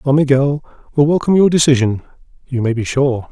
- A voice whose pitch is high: No, low, 135 Hz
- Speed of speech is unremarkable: Yes, average, 180 wpm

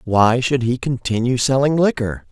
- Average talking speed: Yes, average, 155 wpm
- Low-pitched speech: Yes, low, 125 Hz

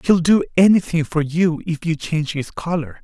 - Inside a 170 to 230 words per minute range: Yes, average, 200 wpm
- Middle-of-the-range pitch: Yes, medium, 160 Hz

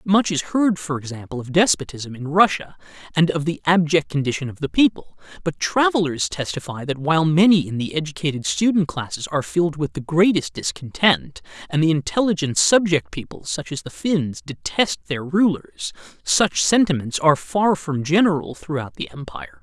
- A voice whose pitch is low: No, medium, 155 Hz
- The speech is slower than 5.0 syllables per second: No, 5.2 syllables/s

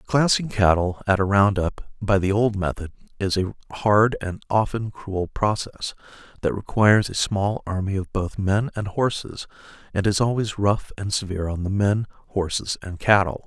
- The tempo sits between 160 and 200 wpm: Yes, average, 175 wpm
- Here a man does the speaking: Yes, male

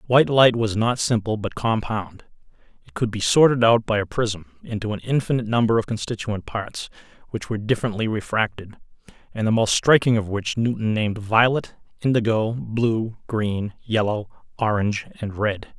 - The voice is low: Yes, low, 110 Hz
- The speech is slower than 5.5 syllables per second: Yes, 5.1 syllables/s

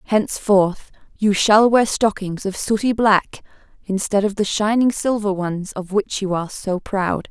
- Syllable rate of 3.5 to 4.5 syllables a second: Yes, 4.3 syllables/s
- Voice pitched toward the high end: Yes, high, 200 Hz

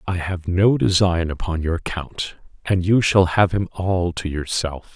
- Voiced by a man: Yes, male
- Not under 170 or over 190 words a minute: Yes, average, 180 wpm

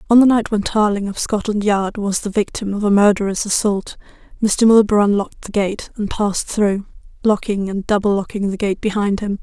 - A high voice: Yes, high, 205 Hz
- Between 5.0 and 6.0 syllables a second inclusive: Yes, 5.4 syllables/s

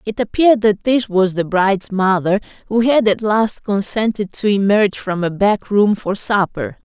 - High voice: Yes, high, 205 Hz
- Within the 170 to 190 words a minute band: Yes, average, 180 wpm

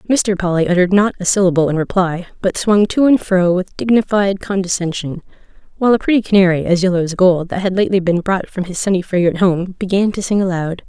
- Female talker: Yes, female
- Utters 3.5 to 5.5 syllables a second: No, 6.1 syllables/s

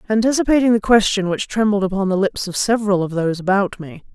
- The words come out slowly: No, fast, 205 wpm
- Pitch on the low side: No, high, 200 Hz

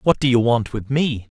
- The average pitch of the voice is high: No, low, 125 Hz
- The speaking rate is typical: No, fast, 260 wpm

